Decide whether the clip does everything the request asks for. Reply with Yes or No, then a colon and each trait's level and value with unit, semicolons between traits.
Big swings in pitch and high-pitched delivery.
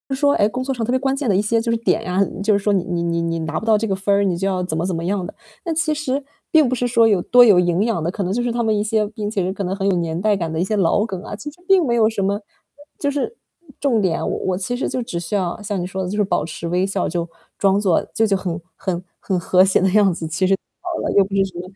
No: average, 4.1 semitones; high, 200 Hz